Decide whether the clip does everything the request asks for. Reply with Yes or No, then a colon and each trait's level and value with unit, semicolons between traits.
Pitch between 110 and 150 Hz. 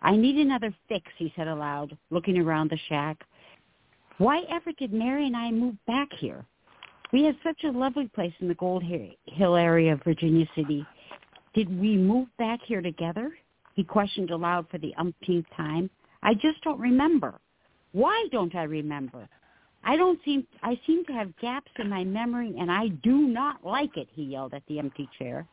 No: high, 195 Hz